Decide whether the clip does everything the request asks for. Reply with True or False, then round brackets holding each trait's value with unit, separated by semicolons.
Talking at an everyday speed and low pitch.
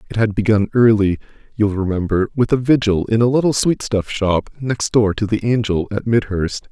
True (195 wpm; 110 Hz)